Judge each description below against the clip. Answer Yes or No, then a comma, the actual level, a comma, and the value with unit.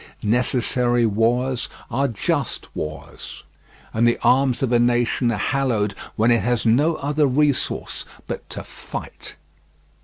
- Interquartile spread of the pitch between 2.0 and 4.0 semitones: Yes, narrow, 2.4 semitones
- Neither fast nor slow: No, slow, 130 wpm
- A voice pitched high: No, low, 120 Hz